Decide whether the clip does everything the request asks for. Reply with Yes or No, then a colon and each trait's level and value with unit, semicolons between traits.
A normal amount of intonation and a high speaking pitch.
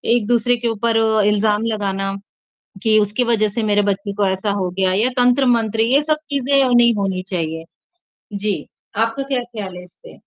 Yes: average, 3.3 semitones; high, 215 Hz